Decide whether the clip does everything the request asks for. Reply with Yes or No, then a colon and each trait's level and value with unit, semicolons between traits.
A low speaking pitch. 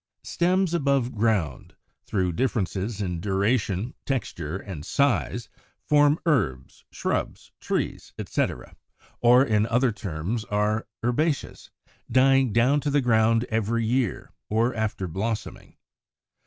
Yes: low, 115 Hz